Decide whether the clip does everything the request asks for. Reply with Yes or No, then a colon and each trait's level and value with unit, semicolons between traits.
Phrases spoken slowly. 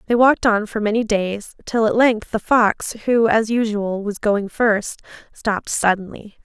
No: average, 175 wpm